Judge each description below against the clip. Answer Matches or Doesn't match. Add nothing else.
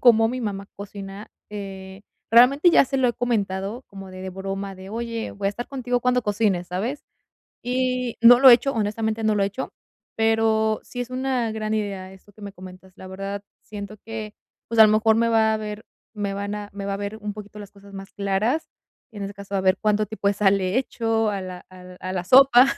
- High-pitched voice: Matches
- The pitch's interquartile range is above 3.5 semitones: Doesn't match